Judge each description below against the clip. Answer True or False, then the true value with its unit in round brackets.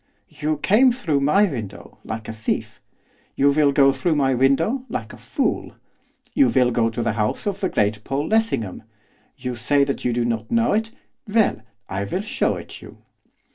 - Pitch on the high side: False (140 Hz)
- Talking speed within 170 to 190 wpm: True (180 wpm)